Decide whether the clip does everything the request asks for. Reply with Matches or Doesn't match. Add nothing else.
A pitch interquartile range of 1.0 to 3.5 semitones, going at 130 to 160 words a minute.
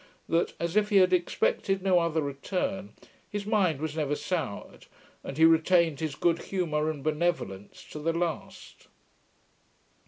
Matches